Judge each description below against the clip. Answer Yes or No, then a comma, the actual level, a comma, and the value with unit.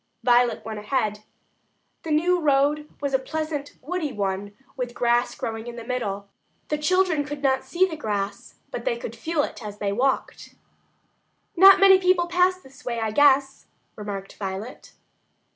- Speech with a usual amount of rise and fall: No, wide, 6.3 semitones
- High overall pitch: Yes, very high, 270 Hz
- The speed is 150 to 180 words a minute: Yes, average, 160 wpm